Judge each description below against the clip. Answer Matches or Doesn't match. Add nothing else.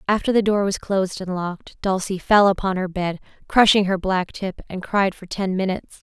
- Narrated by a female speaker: Matches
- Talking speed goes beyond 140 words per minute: Matches